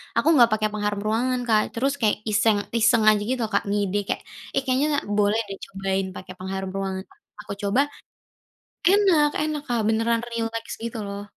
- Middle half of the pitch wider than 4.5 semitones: No, average, 3.0 semitones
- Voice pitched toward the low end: No, high, 220 Hz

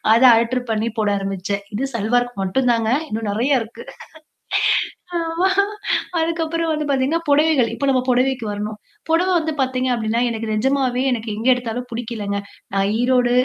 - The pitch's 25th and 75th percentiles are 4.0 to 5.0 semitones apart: No, average, 3.6 semitones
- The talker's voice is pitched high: Yes, high, 245 Hz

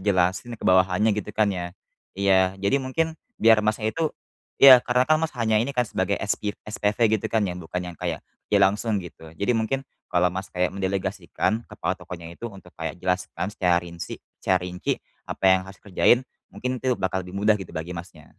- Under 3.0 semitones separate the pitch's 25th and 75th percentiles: No, average, 3.7 semitones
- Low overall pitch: Yes, low, 100 Hz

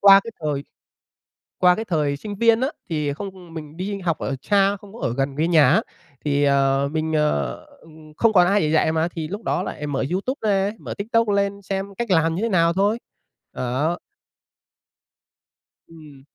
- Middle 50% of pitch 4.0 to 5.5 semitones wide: Yes, average, 5.0 semitones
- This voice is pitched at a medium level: Yes, medium, 170 Hz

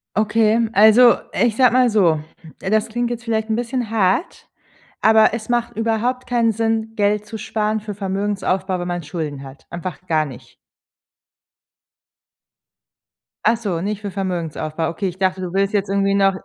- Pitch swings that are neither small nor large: Yes, average, 3.3 semitones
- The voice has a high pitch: Yes, high, 210 Hz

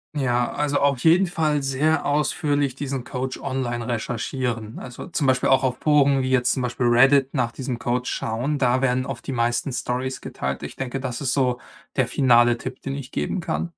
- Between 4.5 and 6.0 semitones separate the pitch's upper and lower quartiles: No, narrow, 2.4 semitones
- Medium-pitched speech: No, low, 130 Hz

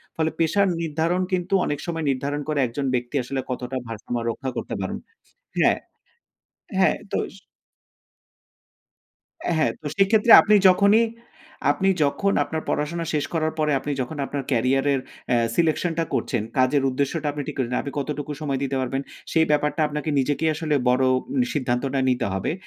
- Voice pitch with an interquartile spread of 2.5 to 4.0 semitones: Yes, average, 3.5 semitones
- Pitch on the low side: No, medium, 145 Hz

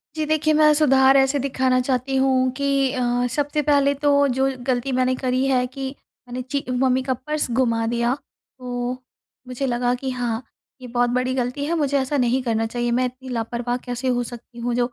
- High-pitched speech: Yes, very high, 255 Hz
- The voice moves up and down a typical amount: No, narrow, 2.0 semitones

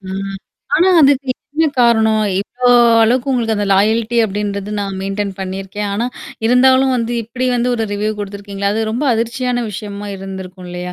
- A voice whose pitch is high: Yes, high, 215 Hz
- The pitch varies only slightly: No, average, 3.4 semitones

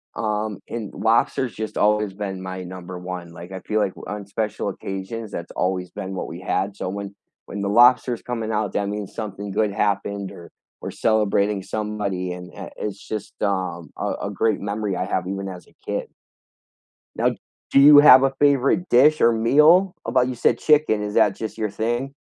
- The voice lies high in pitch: No, low, 105 Hz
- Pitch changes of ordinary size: Yes, average, 3.1 semitones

